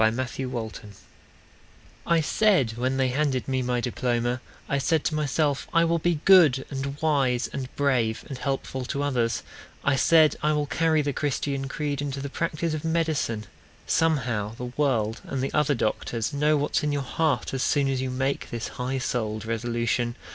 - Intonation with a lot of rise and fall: No, average, 3.4 semitones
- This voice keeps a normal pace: Yes, average, 175 wpm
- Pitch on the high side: No, low, 135 Hz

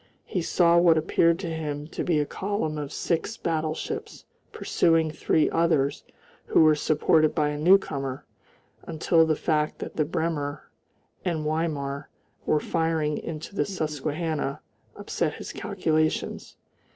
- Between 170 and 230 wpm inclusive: No, slow, 135 wpm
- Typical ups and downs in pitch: No, narrow, 1.8 semitones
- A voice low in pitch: No, medium, 155 Hz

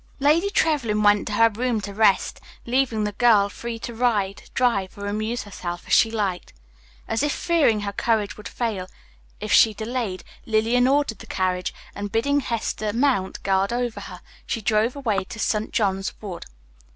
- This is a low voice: No, high, 220 Hz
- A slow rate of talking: No, average, 175 wpm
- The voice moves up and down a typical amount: Yes, average, 3.2 semitones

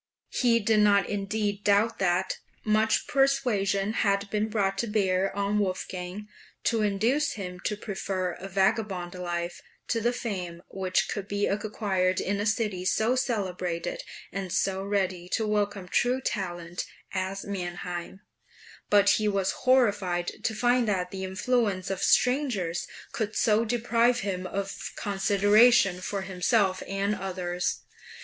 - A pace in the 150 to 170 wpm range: No, average, 140 wpm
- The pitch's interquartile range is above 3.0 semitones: No, average, 2.7 semitones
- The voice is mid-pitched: No, high, 200 Hz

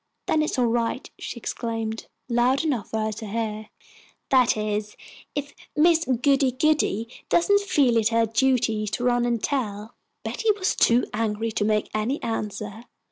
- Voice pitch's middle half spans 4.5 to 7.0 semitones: No, average, 3.6 semitones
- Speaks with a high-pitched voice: Yes, high, 235 Hz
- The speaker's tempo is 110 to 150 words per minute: No, average, 165 wpm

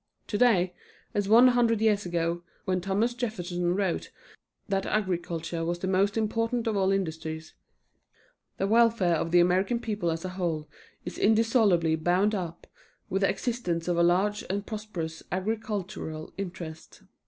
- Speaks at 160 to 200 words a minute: No, average, 145 wpm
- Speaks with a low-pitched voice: No, high, 190 Hz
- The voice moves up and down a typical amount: Yes, average, 3.8 semitones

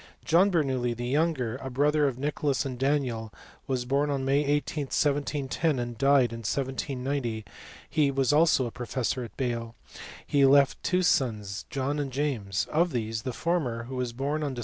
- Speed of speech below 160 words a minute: No, average, 175 wpm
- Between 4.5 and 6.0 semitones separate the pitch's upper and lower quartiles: No, average, 3.2 semitones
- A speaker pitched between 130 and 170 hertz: Yes, low, 135 Hz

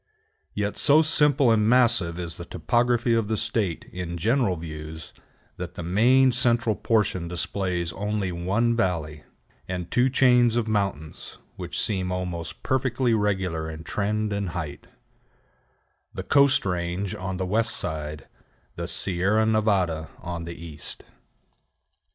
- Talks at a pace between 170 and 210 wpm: No, slow, 135 wpm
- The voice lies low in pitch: Yes, low, 100 Hz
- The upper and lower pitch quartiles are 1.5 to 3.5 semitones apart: No, average, 5.0 semitones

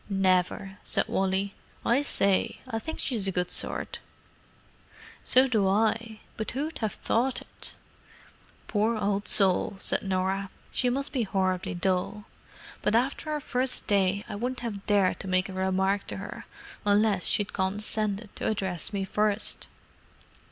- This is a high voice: Yes, high, 205 Hz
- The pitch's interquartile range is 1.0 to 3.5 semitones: Yes, average, 2.8 semitones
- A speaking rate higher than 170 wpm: No, average, 150 wpm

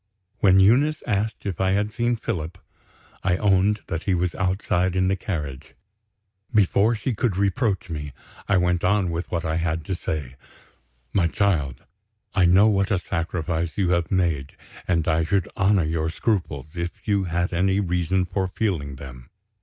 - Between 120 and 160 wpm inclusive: No, average, 170 wpm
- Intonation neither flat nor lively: Yes, average, 3.3 semitones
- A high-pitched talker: No, very low, 90 Hz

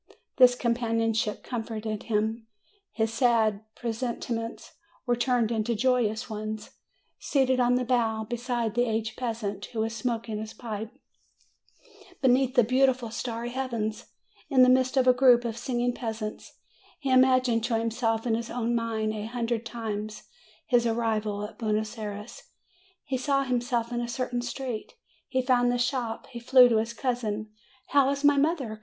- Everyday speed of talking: Yes, average, 165 wpm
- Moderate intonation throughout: No, narrow, 2.2 semitones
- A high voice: Yes, high, 235 Hz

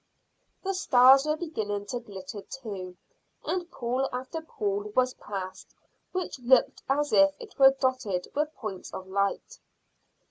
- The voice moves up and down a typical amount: No, wide, 6.8 semitones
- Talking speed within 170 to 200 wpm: No, average, 140 wpm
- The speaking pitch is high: Yes, very high, 260 Hz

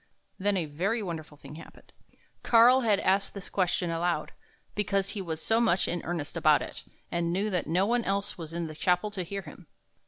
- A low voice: No, medium, 185 Hz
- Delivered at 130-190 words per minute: No, average, 200 wpm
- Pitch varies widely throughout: No, average, 3.3 semitones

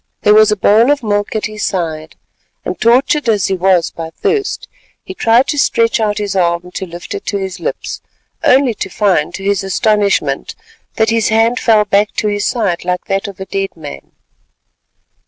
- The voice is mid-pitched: No, high, 205 Hz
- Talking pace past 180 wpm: Yes, average, 190 wpm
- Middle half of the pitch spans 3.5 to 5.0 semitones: No, average, 3.1 semitones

